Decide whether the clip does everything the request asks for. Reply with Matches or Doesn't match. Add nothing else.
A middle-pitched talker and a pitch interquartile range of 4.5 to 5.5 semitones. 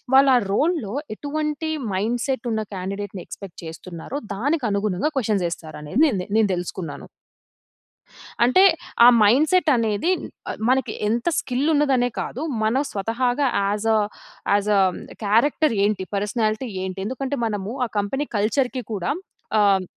Doesn't match